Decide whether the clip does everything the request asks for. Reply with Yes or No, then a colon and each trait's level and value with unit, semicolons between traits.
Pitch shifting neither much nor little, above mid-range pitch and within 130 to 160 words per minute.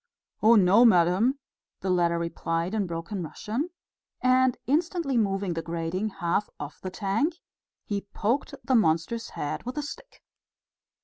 No: wide, 6.6 semitones; high, 205 Hz; average, 140 wpm